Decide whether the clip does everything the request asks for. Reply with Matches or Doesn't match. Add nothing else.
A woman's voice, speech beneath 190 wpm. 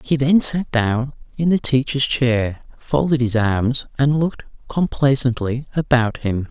Doesn't match